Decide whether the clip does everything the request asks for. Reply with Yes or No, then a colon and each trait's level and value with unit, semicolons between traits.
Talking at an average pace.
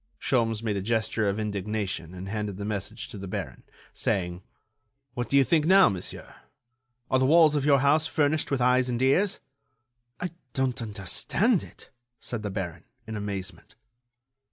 Yes: average, 165 wpm